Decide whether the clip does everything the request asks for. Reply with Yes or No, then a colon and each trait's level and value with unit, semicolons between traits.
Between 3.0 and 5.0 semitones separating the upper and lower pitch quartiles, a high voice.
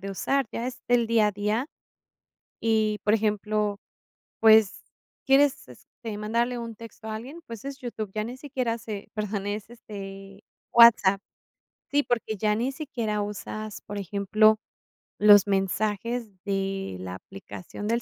No: narrow, 2.4 semitones; high, 215 Hz